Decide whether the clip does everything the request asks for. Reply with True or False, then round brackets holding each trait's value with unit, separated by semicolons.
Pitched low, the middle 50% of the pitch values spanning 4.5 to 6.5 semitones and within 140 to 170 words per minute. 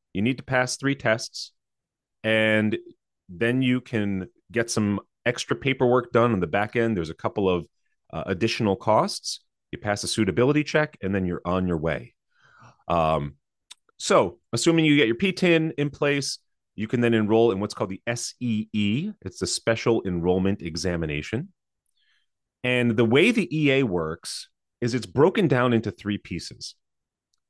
True (115 Hz; 5.0 semitones; 160 wpm)